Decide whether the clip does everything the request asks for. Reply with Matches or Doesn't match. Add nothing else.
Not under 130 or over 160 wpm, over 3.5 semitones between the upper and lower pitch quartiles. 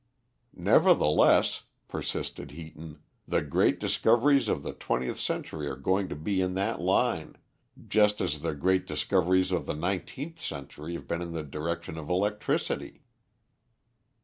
Matches